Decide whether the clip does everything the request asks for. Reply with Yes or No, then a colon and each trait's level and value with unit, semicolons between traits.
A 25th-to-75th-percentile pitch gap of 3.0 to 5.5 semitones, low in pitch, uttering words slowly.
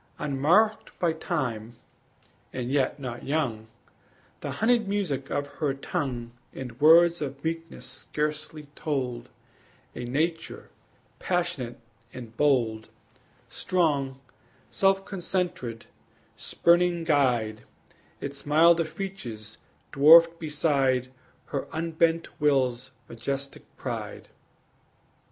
No: average, 4.7 semitones; medium, 145 Hz; slow, 90 wpm